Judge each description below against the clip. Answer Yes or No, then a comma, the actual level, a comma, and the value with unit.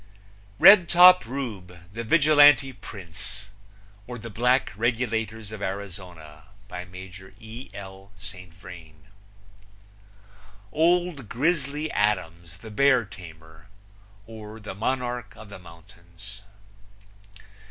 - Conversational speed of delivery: No, slow, 100 wpm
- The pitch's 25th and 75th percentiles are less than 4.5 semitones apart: No, average, 5.2 semitones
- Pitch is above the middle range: No, low, 105 Hz